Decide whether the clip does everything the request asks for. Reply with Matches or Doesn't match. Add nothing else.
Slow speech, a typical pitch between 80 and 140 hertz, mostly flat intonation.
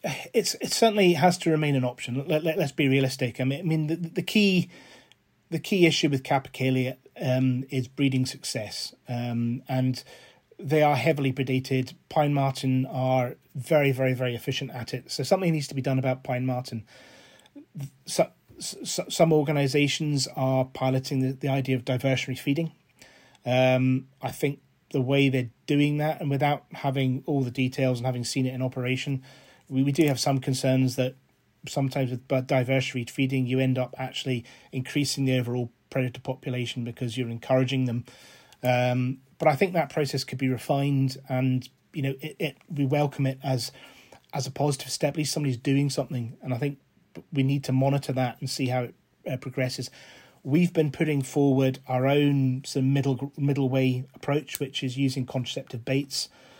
Doesn't match